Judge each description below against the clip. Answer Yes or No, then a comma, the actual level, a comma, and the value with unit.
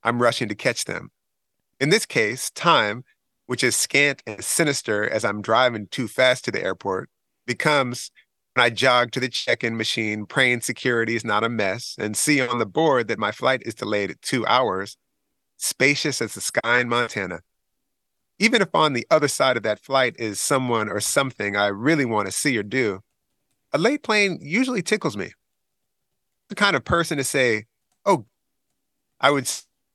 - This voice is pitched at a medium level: No, low, 120 Hz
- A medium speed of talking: Yes, average, 180 wpm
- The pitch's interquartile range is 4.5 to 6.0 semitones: No, average, 4.1 semitones